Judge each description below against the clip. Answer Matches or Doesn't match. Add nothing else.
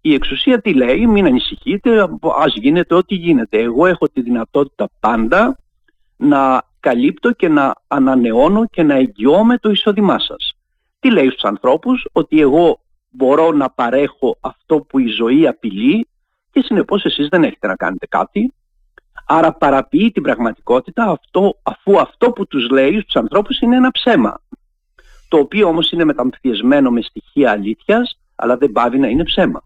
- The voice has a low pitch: Doesn't match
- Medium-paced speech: Matches